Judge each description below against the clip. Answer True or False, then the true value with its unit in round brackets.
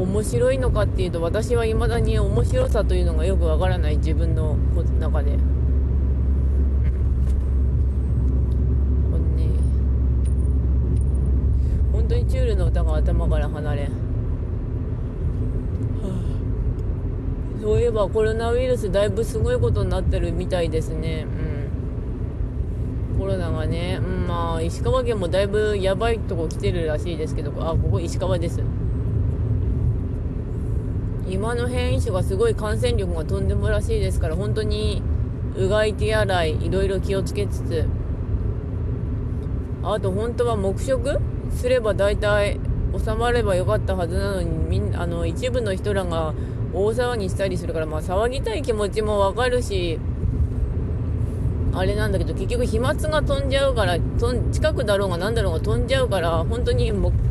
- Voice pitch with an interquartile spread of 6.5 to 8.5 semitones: True (7.4 semitones)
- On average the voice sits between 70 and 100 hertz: True (95 Hz)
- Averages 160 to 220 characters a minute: False (280 characters per minute)